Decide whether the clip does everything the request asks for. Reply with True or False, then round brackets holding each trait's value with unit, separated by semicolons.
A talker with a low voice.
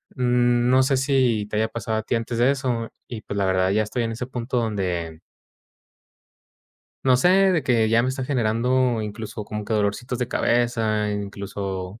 True (115 Hz)